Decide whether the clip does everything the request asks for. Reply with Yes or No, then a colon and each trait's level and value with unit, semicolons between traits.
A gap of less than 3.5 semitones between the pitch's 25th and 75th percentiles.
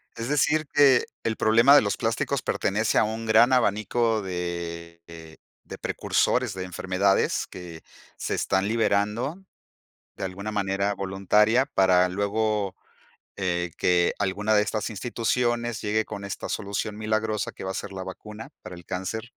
Yes: average, 3.0 semitones